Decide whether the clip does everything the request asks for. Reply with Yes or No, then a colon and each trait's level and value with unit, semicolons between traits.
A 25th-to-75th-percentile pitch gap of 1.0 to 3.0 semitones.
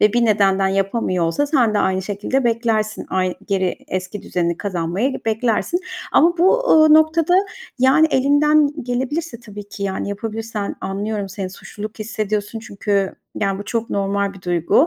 No: average, 4.6 semitones